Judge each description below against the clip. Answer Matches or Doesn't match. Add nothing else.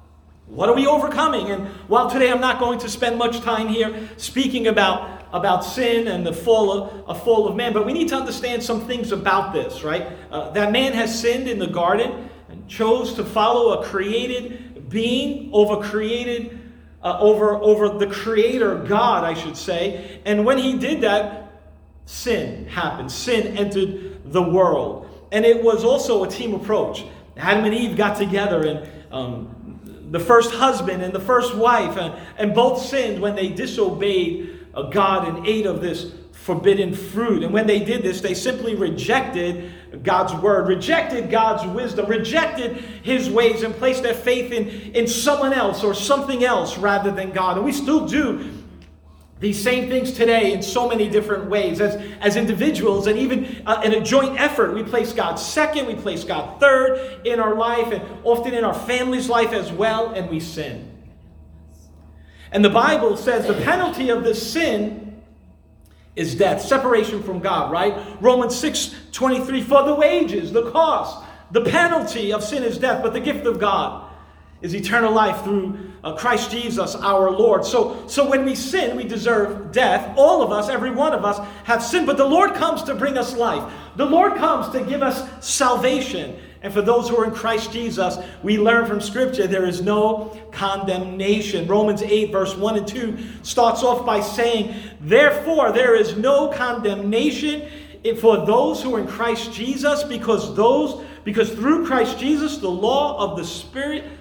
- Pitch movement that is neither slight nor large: Matches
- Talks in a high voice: Matches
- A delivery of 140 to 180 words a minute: Matches